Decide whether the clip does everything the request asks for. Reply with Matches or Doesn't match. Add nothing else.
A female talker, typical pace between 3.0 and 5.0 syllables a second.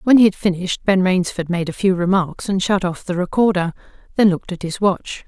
Doesn't match